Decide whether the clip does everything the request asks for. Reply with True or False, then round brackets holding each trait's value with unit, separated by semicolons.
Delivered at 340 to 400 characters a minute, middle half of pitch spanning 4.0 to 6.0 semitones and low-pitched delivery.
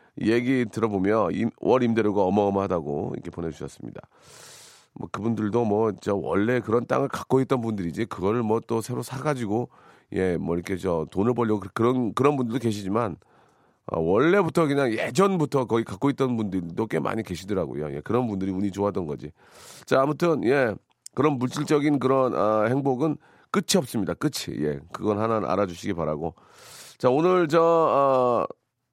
True (350 characters per minute; 5.1 semitones; 115 Hz)